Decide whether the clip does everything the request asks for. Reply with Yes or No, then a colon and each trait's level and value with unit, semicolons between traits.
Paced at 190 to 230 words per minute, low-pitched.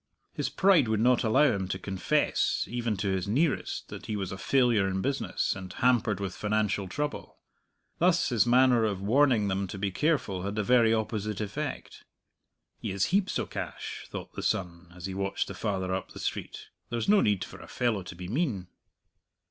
Yes: average, 195 wpm; low, 105 Hz